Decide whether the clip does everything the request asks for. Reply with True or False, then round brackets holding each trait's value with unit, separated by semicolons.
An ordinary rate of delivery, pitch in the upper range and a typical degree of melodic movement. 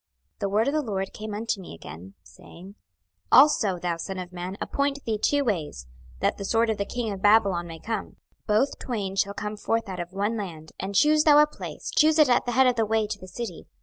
False (245 wpm; 210 Hz; 4.1 semitones)